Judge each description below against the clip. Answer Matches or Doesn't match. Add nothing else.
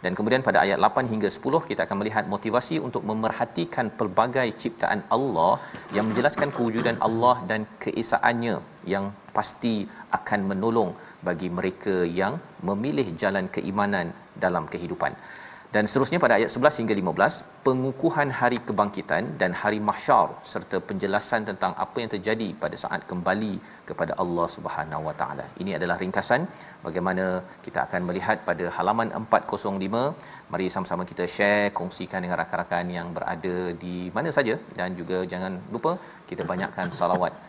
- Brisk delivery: Matches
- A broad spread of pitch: Doesn't match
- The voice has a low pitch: Matches